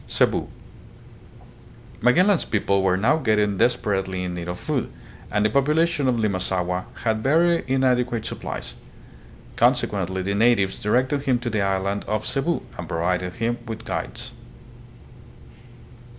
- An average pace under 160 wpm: Yes, slow, 135 wpm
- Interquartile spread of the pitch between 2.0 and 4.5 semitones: No, average, 5.1 semitones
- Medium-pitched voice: No, low, 110 Hz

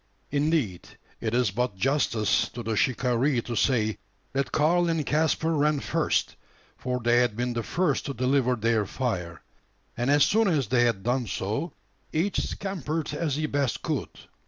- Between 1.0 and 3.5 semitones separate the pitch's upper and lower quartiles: No, average, 4.4 semitones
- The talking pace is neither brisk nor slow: Yes, average, 165 wpm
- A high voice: No, low, 130 Hz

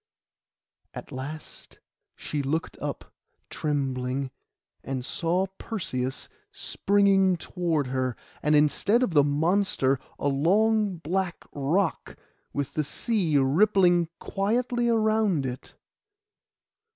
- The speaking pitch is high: No, medium, 165 Hz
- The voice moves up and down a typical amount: No, wide, 6.1 semitones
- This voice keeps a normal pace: No, slow, 100 wpm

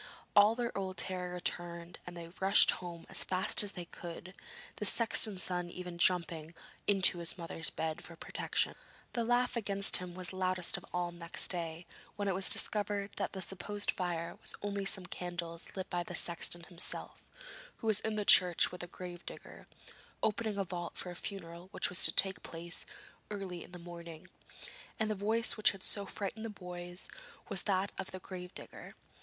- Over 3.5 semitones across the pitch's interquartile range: No, narrow, 2.4 semitones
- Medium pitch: Yes, medium, 180 Hz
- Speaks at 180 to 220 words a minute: Yes, average, 185 wpm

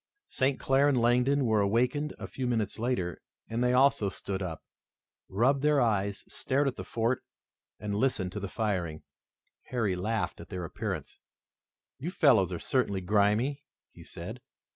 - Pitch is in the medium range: No, low, 115 Hz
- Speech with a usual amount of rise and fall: Yes, average, 4.7 semitones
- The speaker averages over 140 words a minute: Yes, average, 160 wpm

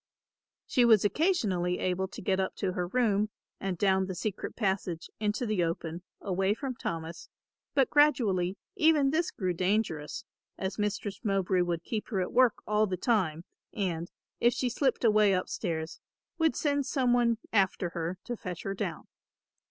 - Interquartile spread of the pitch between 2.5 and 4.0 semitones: No, average, 4.7 semitones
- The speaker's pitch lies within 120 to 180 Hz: No, high, 195 Hz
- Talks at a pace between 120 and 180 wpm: Yes, average, 165 wpm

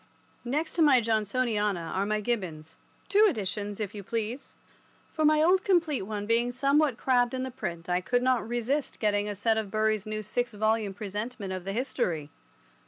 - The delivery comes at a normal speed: Yes, average, 180 wpm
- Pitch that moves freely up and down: No, average, 3.9 semitones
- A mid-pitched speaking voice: No, high, 220 Hz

